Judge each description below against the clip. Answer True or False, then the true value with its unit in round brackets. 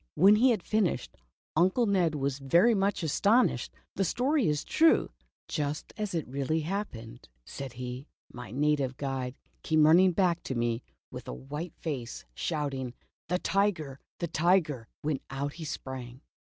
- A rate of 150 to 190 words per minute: True (165 wpm)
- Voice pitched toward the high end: False (150 Hz)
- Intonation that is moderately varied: False (5.8 semitones)